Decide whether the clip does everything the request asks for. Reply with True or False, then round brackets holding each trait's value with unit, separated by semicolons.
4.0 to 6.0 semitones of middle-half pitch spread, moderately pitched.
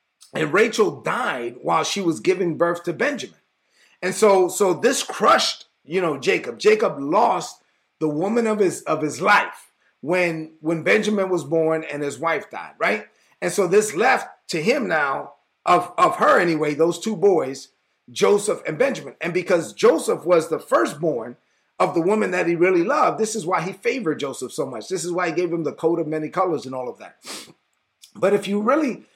True (4.3 semitones; 180 Hz)